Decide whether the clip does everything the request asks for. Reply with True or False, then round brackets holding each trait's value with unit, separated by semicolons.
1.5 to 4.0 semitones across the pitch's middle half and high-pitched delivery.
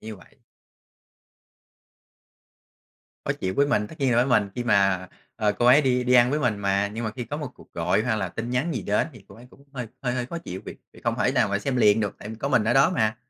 False (3.5 semitones; 120 Hz)